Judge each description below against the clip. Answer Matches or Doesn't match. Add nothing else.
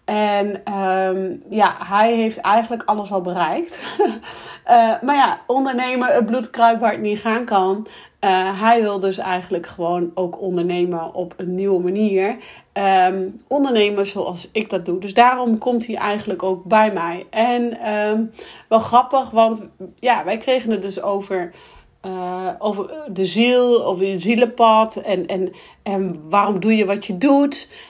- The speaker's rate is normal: Matches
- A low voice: Doesn't match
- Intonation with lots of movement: Doesn't match